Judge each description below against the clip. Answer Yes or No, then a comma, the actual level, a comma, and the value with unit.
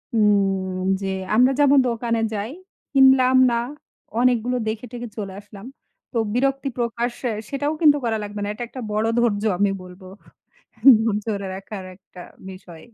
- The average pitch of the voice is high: Yes, high, 225 Hz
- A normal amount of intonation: Yes, average, 3.7 semitones